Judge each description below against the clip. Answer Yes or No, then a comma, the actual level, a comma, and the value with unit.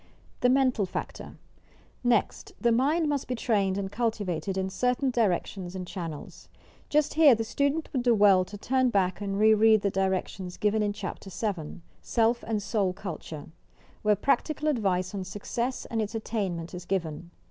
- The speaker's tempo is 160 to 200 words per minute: Yes, average, 170 wpm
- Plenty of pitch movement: No, average, 4.3 semitones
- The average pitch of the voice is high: Yes, high, 210 Hz